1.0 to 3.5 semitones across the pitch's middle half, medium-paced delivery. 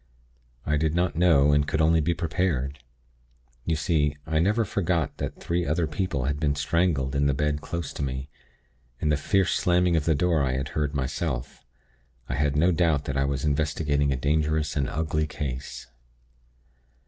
Yes: average, 2.8 semitones; average, 180 wpm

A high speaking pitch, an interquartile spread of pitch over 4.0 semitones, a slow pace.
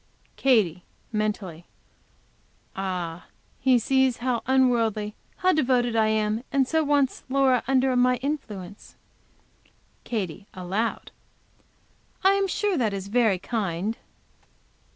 Yes: high, 230 Hz; average, 4.6 semitones; slow, 110 wpm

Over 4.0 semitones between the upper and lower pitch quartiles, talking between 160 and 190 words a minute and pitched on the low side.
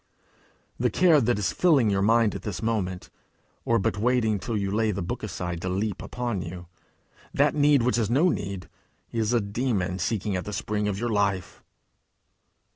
No: average, 3.5 semitones; average, 185 wpm; low, 105 Hz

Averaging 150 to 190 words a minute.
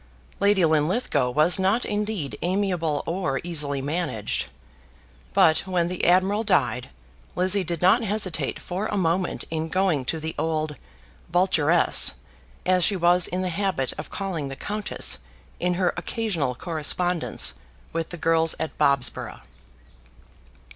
No: slow, 135 wpm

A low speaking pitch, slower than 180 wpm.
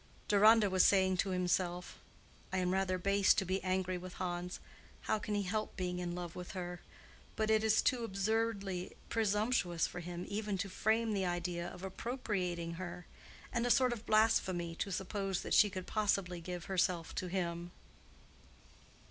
No: medium, 185 Hz; average, 170 wpm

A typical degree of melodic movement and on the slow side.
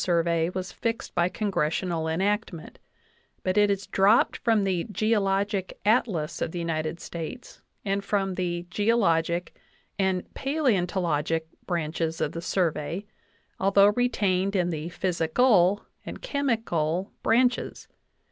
Yes: average, 3.5 semitones; slow, 125 wpm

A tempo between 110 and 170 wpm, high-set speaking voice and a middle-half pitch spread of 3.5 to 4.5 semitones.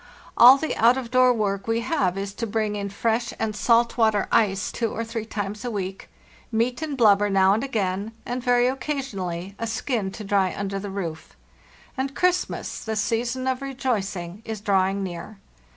No: average, 185 wpm; high, 220 Hz; average, 3.8 semitones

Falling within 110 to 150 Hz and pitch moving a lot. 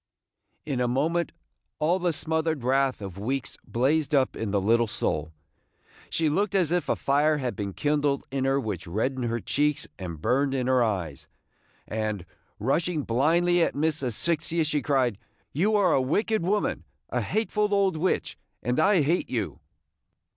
Yes: medium, 140 Hz; wide, 5.7 semitones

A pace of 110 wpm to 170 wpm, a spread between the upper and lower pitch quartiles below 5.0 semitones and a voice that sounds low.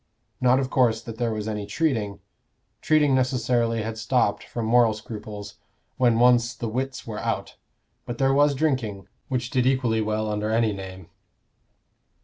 Yes: average, 155 wpm; average, 3.0 semitones; low, 115 Hz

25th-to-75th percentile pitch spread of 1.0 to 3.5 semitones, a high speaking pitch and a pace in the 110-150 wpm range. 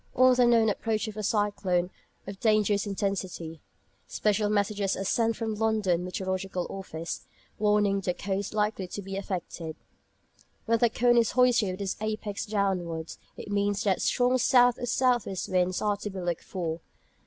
No: average, 2.7 semitones; high, 205 Hz; average, 170 wpm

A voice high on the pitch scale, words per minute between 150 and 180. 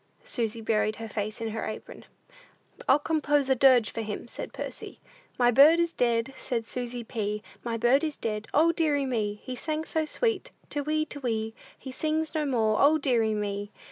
No: high, 245 Hz; average, 190 wpm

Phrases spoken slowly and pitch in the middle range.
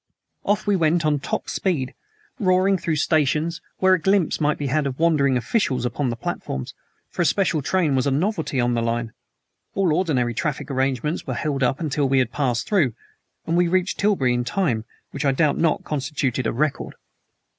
No: average, 190 wpm; medium, 150 Hz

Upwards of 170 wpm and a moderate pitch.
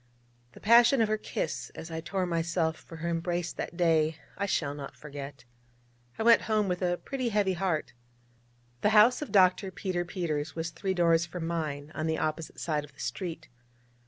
Yes: average, 190 wpm; medium, 170 Hz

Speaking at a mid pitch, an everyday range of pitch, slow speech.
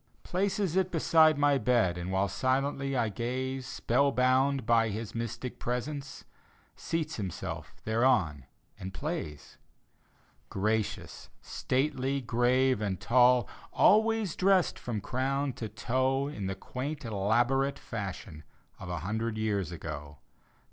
No: low, 125 Hz; average, 4.7 semitones; slow, 120 wpm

